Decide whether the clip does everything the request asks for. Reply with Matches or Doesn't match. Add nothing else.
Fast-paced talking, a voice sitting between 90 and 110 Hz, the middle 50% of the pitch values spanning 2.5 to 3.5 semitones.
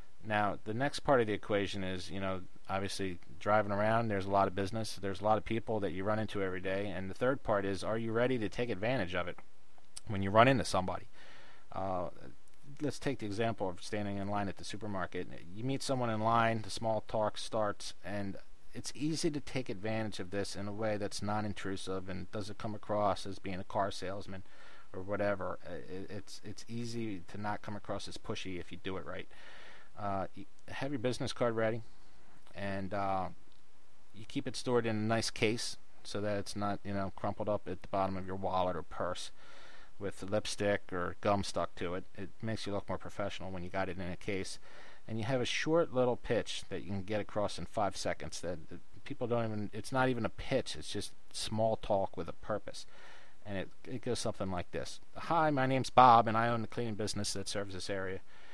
Matches